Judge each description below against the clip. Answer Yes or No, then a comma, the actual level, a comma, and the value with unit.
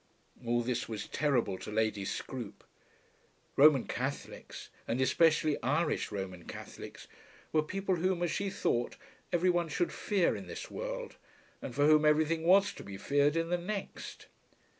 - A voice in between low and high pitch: Yes, medium, 150 Hz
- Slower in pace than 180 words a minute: Yes, average, 155 wpm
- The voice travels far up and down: Yes, wide, 6.4 semitones